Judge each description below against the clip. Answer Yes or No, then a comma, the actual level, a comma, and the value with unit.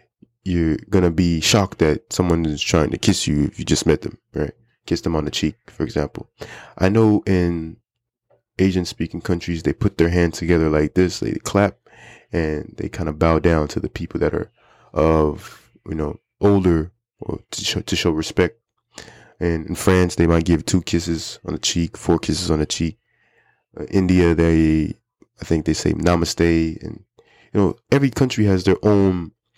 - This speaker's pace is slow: No, average, 190 wpm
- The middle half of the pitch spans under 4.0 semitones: Yes, average, 2.8 semitones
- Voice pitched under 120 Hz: Yes, very low, 85 Hz